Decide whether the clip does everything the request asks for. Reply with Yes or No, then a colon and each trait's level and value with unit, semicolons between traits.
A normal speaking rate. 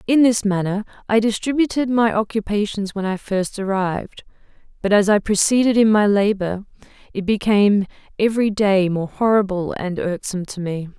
Yes: average, 155 wpm